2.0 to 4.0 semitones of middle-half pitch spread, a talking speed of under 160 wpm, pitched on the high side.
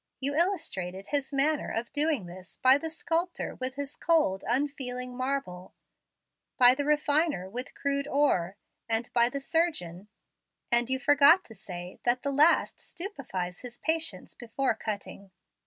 No: average, 5.2 semitones; average, 145 wpm; very high, 265 Hz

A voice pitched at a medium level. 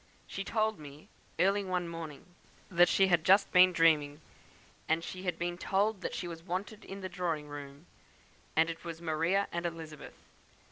Yes: medium, 175 Hz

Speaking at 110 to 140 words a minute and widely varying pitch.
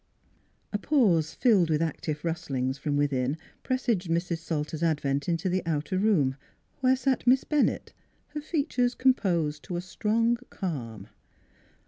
Yes: slow, 135 wpm; wide, 7.7 semitones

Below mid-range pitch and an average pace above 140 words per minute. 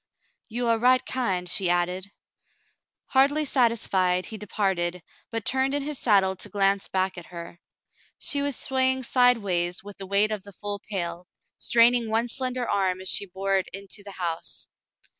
No: high, 200 Hz; average, 165 wpm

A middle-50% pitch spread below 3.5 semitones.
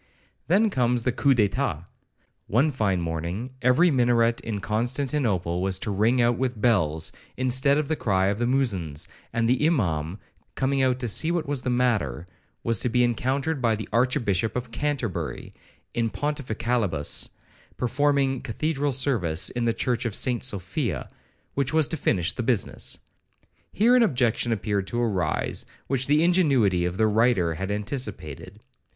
No: average, 5.0 semitones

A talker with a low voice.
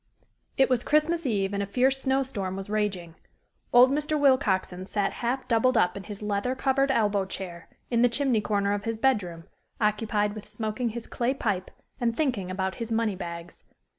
No: high, 215 Hz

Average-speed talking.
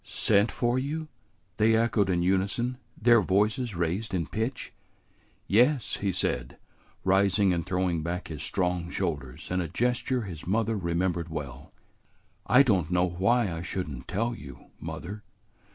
Yes: average, 150 wpm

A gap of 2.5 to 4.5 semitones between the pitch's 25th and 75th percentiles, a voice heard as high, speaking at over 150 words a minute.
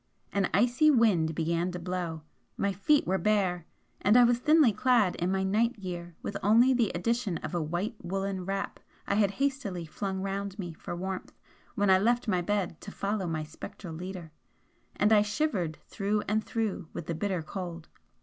Yes: average, 3.6 semitones; high, 195 Hz; average, 185 wpm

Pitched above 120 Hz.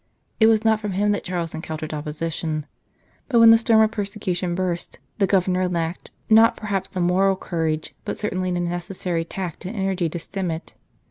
Yes: medium, 185 Hz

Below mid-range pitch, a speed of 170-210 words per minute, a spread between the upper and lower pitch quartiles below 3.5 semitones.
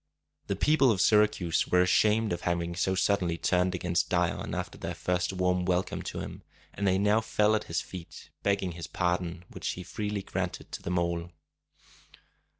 Yes: very low, 90 Hz; average, 175 wpm; narrow, 2.5 semitones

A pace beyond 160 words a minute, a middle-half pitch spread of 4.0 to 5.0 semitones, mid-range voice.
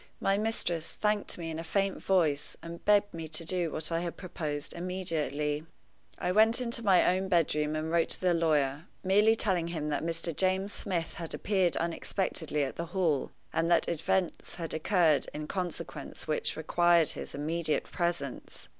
No: average, 170 wpm; average, 3.1 semitones; medium, 170 Hz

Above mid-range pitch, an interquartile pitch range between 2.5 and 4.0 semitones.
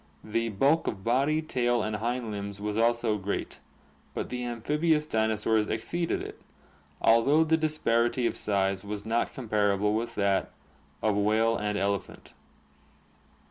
No: low, 115 Hz; average, 2.9 semitones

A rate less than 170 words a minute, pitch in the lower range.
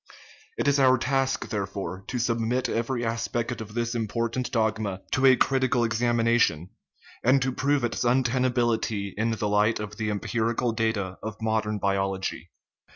Yes: average, 155 wpm; low, 115 Hz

